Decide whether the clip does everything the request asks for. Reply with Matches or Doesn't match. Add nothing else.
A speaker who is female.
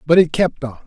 Doesn't match